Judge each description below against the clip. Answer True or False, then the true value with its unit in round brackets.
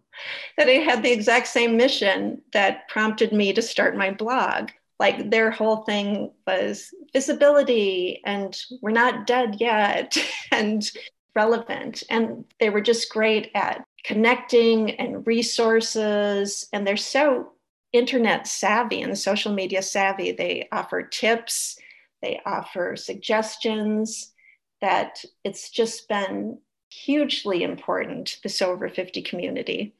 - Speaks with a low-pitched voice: False (225 Hz)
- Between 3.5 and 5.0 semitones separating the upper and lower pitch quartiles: False (3.0 semitones)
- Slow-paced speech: True (120 wpm)